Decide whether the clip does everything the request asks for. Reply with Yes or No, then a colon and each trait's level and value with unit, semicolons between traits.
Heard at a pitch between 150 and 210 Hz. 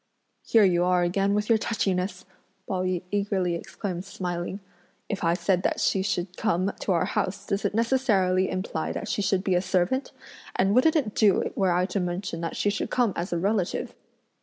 Yes: high, 190 Hz